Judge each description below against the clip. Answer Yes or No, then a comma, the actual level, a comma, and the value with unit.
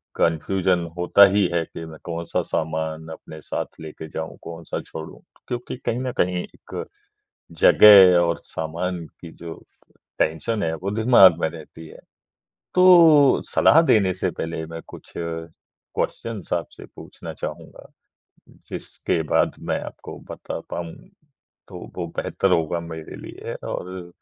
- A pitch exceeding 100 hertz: No, very low, 85 Hz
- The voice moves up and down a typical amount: Yes, average, 3.1 semitones